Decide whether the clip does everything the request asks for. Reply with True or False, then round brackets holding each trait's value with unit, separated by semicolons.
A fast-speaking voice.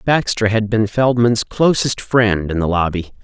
False (165 wpm)